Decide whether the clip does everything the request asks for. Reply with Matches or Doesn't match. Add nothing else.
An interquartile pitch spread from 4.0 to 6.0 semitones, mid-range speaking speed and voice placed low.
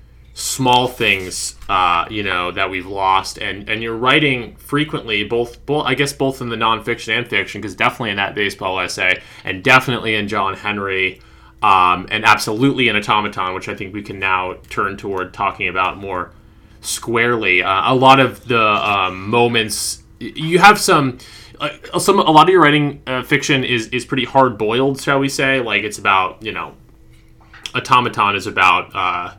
Matches